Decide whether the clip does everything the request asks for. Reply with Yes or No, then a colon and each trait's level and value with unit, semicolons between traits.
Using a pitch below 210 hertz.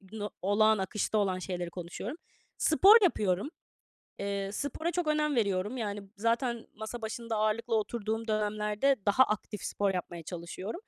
No: high, 215 Hz